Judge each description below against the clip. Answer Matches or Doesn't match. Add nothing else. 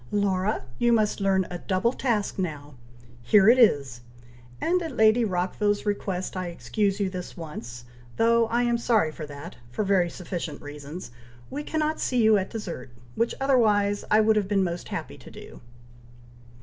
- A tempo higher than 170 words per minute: Doesn't match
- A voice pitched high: Matches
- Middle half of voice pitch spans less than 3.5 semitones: Doesn't match